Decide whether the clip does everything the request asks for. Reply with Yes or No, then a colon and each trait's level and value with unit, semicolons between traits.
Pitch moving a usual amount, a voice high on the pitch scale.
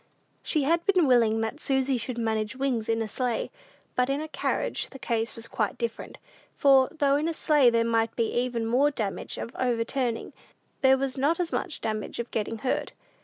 Yes: average, 3.3 semitones; very high, 250 Hz